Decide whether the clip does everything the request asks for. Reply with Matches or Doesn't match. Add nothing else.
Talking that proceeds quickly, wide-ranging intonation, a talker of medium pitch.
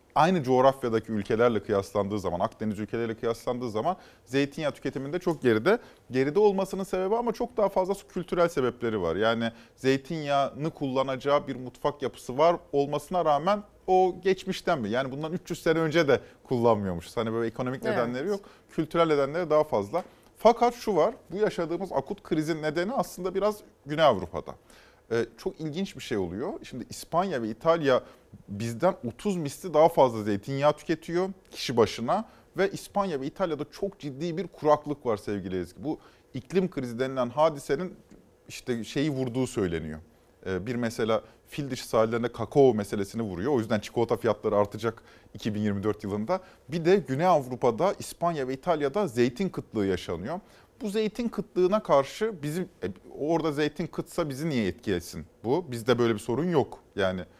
Matches